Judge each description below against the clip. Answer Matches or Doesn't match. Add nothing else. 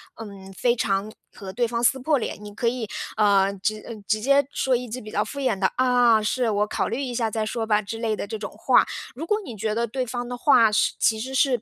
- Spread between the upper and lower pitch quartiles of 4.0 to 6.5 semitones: Doesn't match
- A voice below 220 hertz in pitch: Doesn't match